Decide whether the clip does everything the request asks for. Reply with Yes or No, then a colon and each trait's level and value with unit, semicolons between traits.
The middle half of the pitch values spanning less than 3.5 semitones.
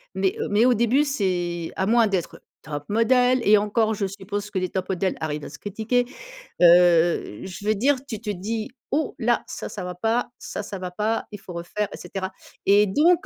No: average, 3.8 semitones